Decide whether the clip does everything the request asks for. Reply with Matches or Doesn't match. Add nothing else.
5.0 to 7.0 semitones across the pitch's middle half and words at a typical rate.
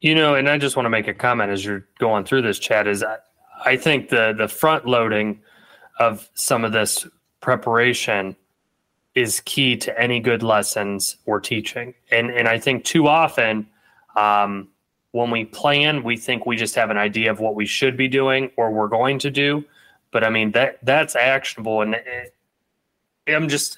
Doesn't match